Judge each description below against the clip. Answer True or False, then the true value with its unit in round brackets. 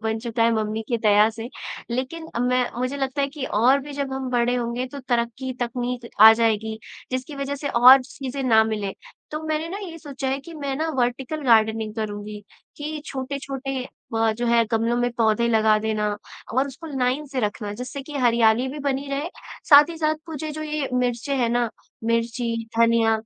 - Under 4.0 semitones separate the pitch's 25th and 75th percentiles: True (3.5 semitones)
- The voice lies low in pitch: False (250 Hz)